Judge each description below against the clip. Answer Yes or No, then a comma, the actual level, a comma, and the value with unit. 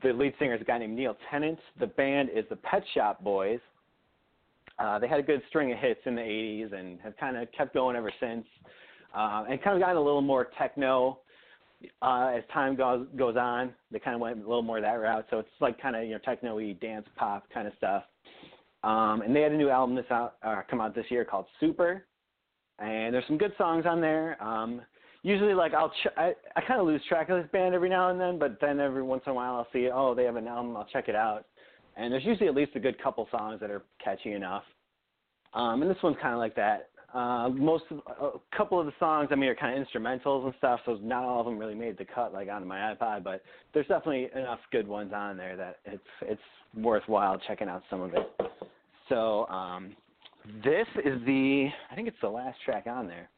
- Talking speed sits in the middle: No, fast, 235 wpm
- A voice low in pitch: Yes, low, 130 Hz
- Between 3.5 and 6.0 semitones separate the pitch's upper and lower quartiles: Yes, average, 4.3 semitones